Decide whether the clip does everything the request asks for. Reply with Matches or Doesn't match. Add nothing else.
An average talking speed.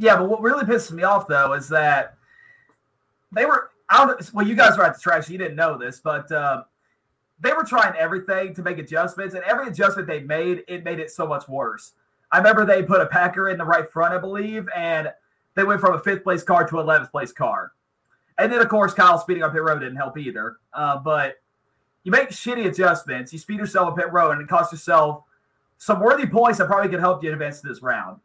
Doesn't match